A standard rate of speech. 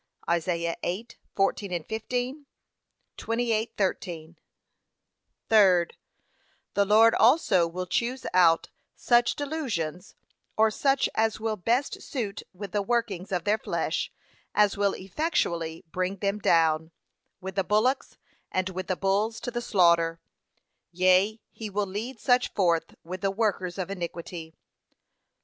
No: slow, 125 wpm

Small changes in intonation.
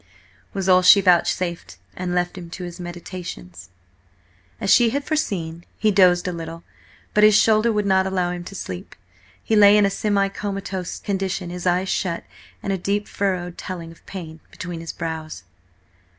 Yes: narrow, 2.3 semitones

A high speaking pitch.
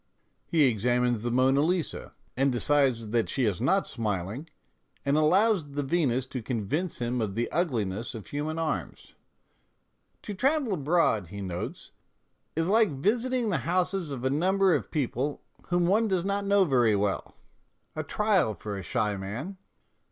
No: medium, 140 Hz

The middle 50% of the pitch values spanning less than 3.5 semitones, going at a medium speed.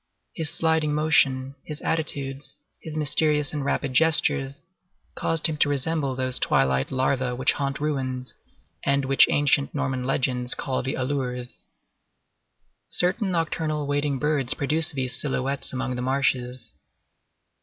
No: average, 2.7 semitones; slow, 130 wpm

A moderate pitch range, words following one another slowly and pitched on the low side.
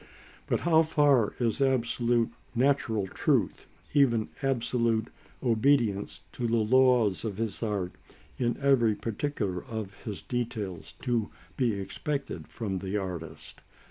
Yes: average, 3.8 semitones; slow, 120 wpm; low, 115 Hz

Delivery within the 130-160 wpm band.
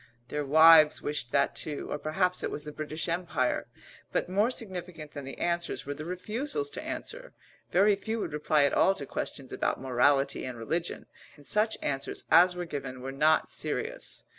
No: average, 185 wpm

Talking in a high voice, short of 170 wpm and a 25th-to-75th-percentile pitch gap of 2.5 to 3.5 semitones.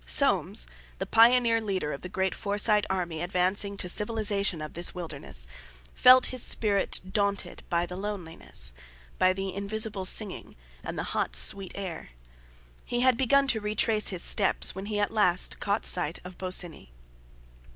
Yes: high, 200 Hz; average, 160 wpm; average, 3.0 semitones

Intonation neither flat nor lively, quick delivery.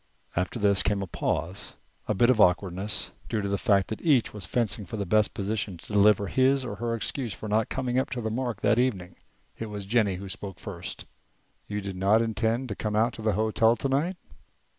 Yes: average, 3.0 semitones; fast, 215 wpm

